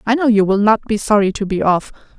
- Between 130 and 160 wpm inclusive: No, fast, 275 wpm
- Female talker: Yes, female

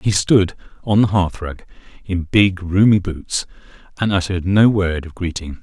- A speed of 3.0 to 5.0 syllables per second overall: Yes, 4.6 syllables/s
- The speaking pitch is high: No, very low, 95 Hz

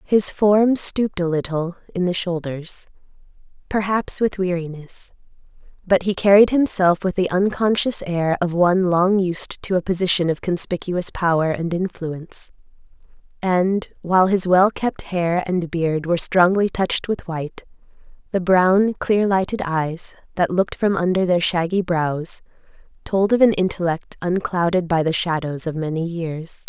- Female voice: Yes, female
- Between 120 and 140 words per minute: No, average, 150 wpm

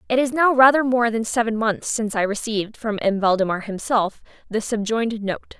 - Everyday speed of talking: Yes, average, 195 wpm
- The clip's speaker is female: Yes, female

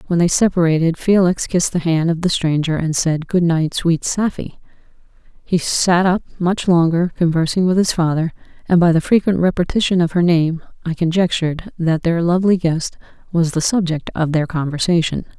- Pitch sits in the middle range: Yes, medium, 170 Hz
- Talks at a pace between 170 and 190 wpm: Yes, average, 175 wpm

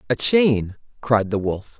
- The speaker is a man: Yes, male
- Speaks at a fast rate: No, average, 170 wpm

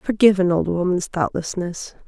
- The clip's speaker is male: No, female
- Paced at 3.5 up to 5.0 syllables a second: No, 5.2 syllables/s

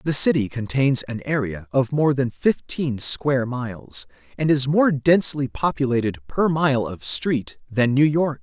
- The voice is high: No, low, 135 Hz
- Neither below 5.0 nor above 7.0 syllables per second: No, 4.3 syllables/s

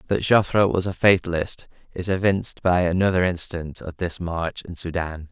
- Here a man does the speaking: Yes, male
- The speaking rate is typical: Yes, average, 170 wpm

